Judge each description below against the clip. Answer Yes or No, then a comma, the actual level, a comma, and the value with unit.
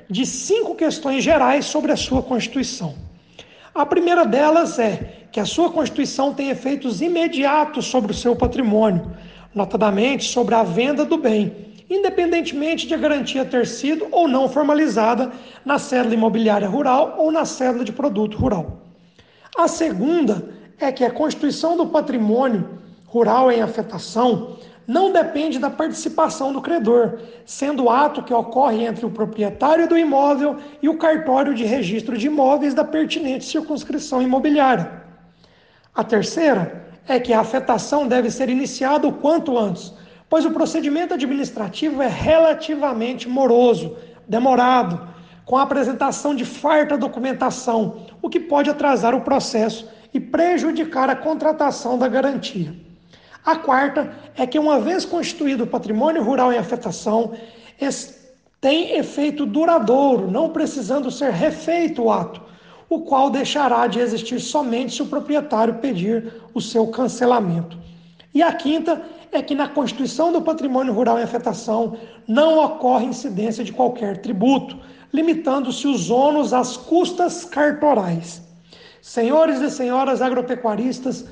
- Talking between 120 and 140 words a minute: Yes, average, 135 wpm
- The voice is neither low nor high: No, very high, 260 Hz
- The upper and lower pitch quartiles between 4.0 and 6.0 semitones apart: Yes, average, 4.4 semitones